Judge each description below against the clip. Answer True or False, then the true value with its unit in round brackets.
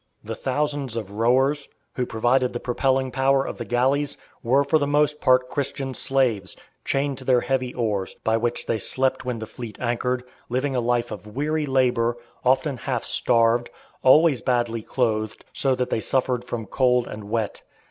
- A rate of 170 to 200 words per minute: True (175 wpm)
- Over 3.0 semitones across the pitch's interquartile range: False (2.4 semitones)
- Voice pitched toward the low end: True (125 Hz)